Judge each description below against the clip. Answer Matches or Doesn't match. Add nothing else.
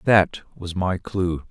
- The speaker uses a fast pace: Doesn't match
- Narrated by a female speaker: Doesn't match